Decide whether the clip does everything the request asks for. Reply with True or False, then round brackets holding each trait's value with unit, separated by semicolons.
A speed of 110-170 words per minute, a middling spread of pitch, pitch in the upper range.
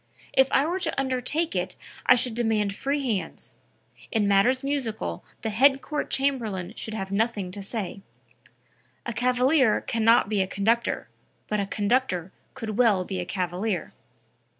True (155 wpm; 4.6 semitones; 225 Hz)